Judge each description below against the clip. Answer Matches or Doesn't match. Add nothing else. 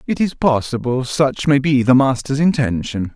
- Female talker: Doesn't match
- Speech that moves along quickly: Doesn't match